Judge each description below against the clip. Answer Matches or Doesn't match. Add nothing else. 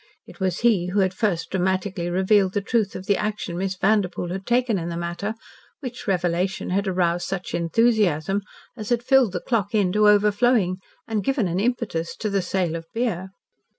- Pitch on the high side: Matches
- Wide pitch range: Doesn't match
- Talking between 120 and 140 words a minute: Doesn't match